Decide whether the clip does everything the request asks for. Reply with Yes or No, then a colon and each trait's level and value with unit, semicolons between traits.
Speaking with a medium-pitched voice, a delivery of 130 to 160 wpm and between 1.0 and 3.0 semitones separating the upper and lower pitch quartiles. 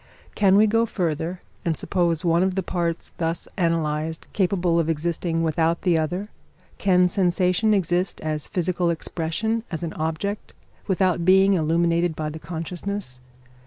Yes: medium, 170 Hz; average, 145 wpm; narrow, 2.5 semitones